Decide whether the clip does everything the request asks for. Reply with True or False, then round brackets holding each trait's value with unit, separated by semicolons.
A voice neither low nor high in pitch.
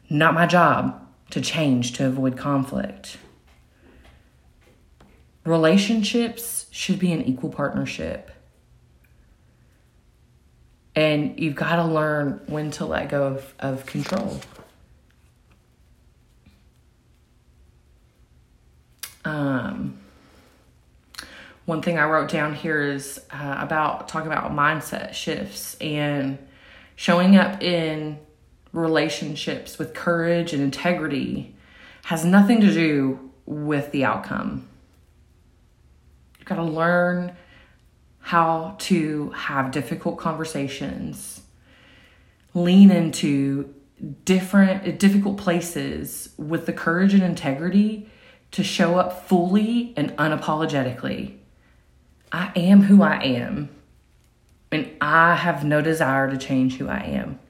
True (150 Hz)